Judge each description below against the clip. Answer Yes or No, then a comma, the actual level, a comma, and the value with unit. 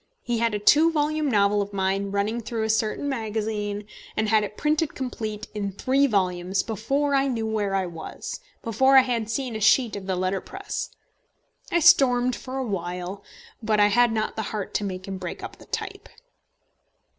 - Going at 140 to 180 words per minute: No, average, 190 wpm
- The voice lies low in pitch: No, high, 220 Hz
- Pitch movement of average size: Yes, average, 4.1 semitones